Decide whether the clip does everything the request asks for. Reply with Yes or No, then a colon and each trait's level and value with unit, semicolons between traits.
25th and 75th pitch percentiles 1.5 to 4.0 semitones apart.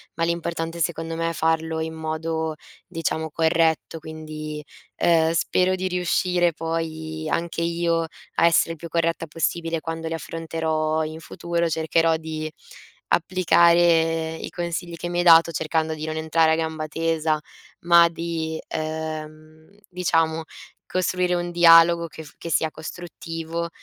No: narrow, 1.0 semitones